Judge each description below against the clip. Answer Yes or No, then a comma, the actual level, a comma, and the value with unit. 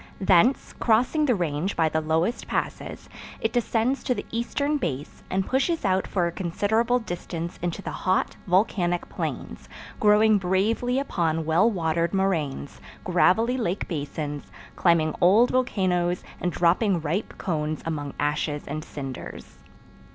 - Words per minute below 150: Yes, slow, 135 wpm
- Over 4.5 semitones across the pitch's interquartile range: Yes, wide, 5.5 semitones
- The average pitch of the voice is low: No, medium, 180 Hz